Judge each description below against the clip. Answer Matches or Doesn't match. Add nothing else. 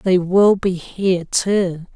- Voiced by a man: Matches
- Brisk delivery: Doesn't match